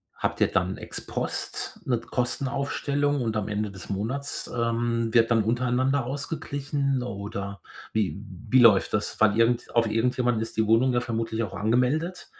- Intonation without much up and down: No, average, 3.1 semitones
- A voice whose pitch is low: Yes, low, 120 Hz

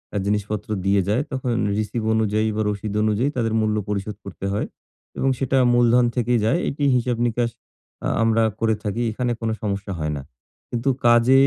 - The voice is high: No, low, 110 Hz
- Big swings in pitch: No, narrow, 2.6 semitones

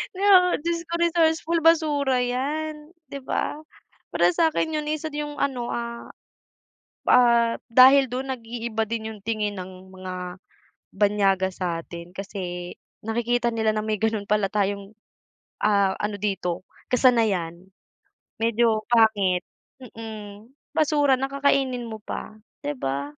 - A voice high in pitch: Yes, high, 225 Hz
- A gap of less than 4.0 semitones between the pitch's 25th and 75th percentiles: No, wide, 5.5 semitones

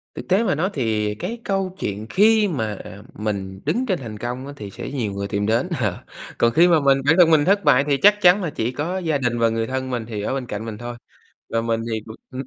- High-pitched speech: No, low, 130 Hz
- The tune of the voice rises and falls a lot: Yes, wide, 7.7 semitones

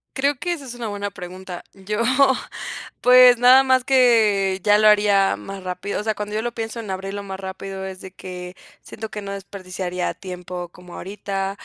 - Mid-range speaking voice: No, high, 200 Hz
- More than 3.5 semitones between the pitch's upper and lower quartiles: No, average, 2.9 semitones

